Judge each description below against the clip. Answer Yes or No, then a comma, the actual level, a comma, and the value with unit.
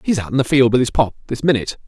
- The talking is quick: Yes, fast, 320 wpm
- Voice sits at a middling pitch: No, low, 125 Hz